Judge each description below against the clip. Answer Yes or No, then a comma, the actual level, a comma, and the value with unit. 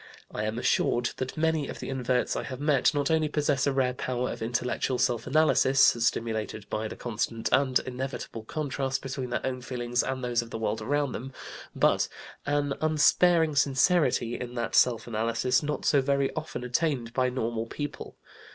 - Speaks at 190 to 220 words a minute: No, average, 180 wpm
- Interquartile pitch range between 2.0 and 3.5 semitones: Yes, average, 3.1 semitones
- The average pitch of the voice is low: Yes, low, 130 Hz